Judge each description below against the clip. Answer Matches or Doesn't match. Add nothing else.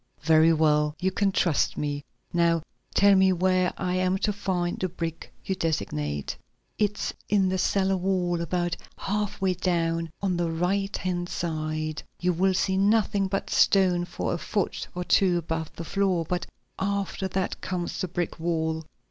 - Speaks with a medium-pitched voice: Matches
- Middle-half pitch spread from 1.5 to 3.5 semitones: Matches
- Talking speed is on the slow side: Doesn't match